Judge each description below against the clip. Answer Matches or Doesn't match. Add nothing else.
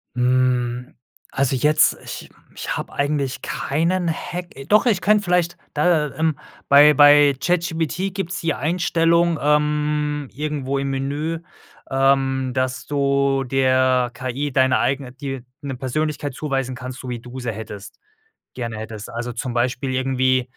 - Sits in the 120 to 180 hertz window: Matches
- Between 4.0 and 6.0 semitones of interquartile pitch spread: Doesn't match